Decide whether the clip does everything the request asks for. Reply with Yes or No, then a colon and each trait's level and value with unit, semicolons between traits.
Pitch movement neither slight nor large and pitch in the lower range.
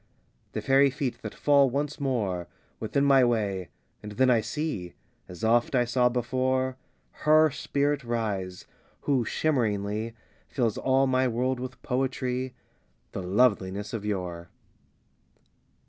Yes: average, 4.1 semitones; low, 125 Hz